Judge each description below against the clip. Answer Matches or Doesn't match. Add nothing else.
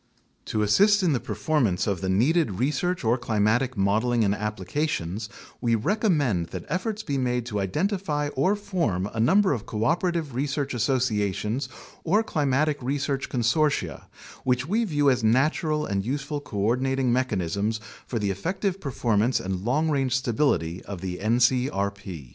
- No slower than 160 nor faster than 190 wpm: Doesn't match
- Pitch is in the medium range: Doesn't match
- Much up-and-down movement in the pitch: Matches